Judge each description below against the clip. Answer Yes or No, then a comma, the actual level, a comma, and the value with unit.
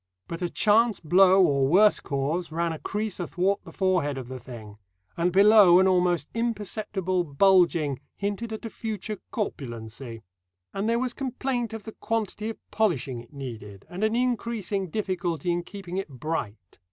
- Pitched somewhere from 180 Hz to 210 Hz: Yes, medium, 185 Hz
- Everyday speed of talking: Yes, average, 165 wpm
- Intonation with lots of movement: Yes, wide, 6.5 semitones